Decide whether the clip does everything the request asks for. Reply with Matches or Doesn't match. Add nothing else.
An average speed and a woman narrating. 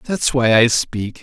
Doesn't match